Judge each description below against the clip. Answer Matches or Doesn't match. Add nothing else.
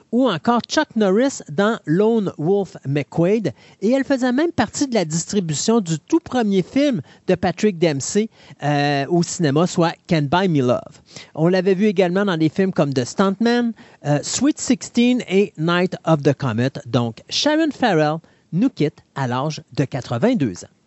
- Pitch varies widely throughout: Matches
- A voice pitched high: Doesn't match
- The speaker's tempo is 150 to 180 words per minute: Matches